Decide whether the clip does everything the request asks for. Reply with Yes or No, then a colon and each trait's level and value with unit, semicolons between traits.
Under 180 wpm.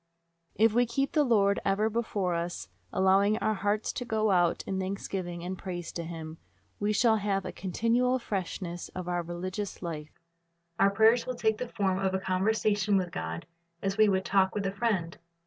No: average, 185 wpm